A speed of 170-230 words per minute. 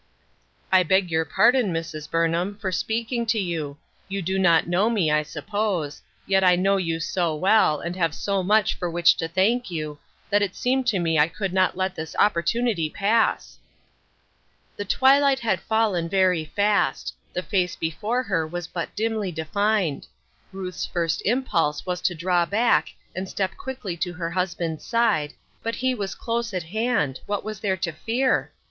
Yes: average, 175 wpm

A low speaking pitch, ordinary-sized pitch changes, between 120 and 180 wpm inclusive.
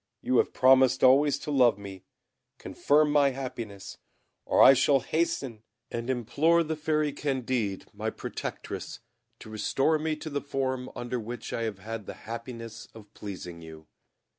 Yes: low, 130 Hz; average, 4.3 semitones; average, 155 wpm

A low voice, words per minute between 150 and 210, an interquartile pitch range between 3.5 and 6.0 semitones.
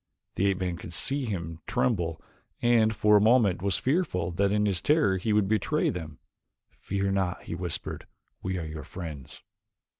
Yes: very low, 95 Hz; average, 175 wpm; average, 3.8 semitones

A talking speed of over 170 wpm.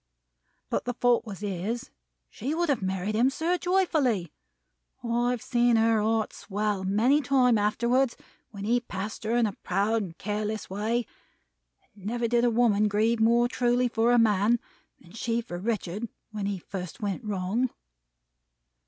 No: average, 160 wpm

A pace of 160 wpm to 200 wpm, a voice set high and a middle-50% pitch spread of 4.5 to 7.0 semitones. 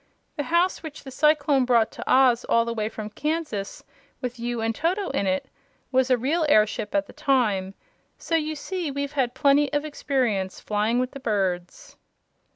Yes: average, 180 wpm; very high, 260 Hz; average, 5.1 semitones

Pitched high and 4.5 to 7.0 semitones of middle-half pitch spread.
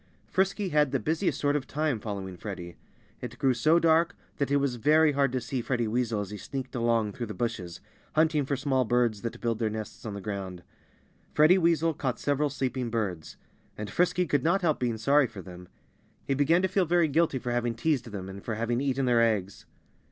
No: low, 125 Hz; wide, 5.5 semitones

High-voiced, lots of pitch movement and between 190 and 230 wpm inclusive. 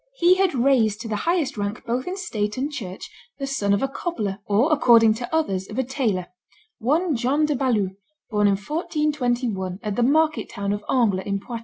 Yes: high, 240 Hz; wide, 6.2 semitones; average, 200 wpm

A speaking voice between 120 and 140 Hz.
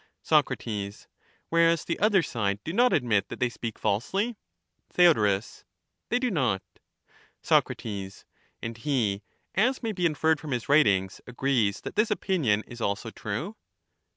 Yes: low, 135 Hz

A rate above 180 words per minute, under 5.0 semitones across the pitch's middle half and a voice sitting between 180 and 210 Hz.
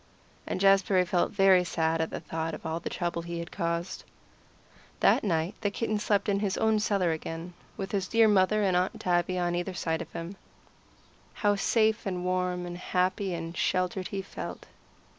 Yes: average, 190 wpm; narrow, 2.6 semitones; medium, 185 Hz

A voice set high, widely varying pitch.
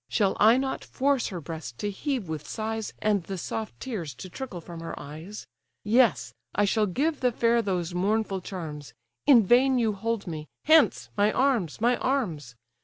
Yes: high, 210 Hz; wide, 5.7 semitones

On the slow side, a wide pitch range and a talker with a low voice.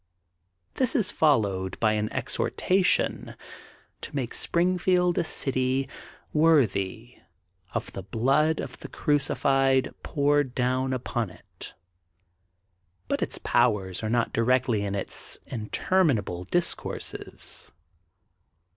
Yes: slow, 105 wpm; wide, 5.8 semitones; low, 130 Hz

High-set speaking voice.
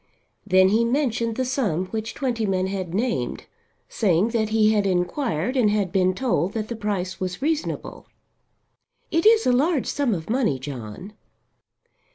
Yes: high, 215 Hz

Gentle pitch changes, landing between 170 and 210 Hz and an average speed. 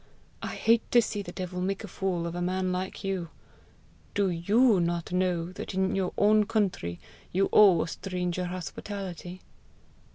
Yes: narrow, 2.0 semitones; medium, 185 Hz; average, 165 wpm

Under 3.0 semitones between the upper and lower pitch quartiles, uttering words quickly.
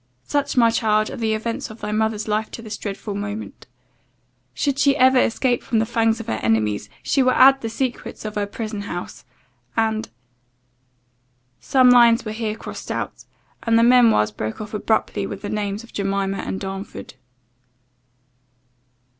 No: narrow, 2.4 semitones; average, 170 wpm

